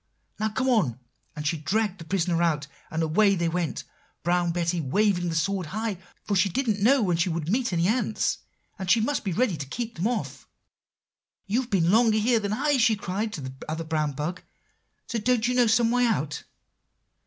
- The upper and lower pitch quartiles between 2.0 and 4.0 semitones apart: No, average, 5.3 semitones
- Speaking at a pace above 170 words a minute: Yes, average, 200 wpm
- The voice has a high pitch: Yes, high, 195 Hz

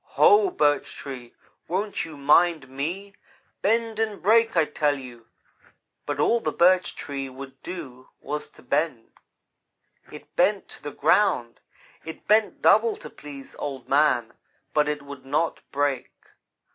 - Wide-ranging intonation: Yes, wide, 6.2 semitones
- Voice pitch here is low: No, medium, 150 Hz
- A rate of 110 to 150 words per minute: Yes, average, 145 wpm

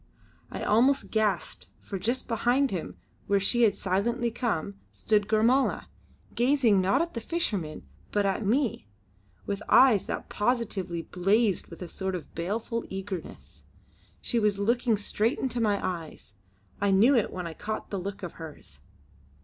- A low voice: No, high, 210 Hz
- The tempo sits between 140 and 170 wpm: Yes, average, 155 wpm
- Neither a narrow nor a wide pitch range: Yes, average, 3.8 semitones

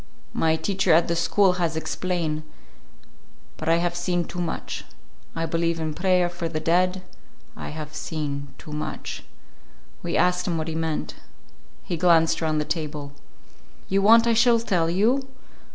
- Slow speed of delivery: No, average, 160 wpm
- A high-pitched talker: No, medium, 170 Hz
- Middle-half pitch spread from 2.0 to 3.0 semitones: Yes, narrow, 2.4 semitones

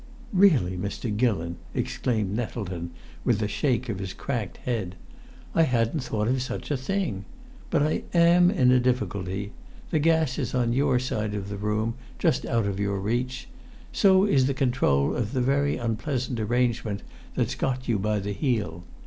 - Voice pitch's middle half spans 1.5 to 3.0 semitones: No, average, 4.5 semitones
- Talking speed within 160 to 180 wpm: Yes, average, 170 wpm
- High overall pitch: No, low, 120 Hz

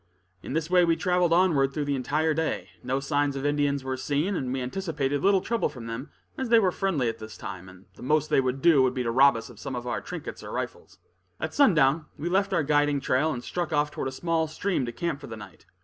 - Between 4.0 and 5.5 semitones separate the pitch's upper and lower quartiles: Yes, average, 4.3 semitones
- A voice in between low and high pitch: Yes, medium, 145 Hz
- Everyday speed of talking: No, fast, 255 wpm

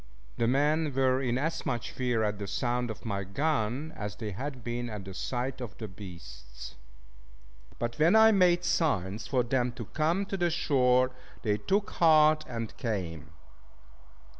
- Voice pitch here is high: No, low, 125 Hz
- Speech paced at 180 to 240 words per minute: No, average, 165 wpm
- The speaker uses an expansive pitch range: Yes, wide, 6.3 semitones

